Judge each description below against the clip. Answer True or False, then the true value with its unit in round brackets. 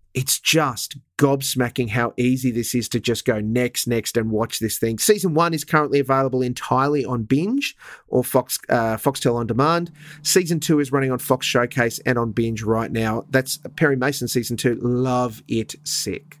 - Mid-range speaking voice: False (130 Hz)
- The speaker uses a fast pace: False (185 wpm)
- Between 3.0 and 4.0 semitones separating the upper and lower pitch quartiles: True (3.5 semitones)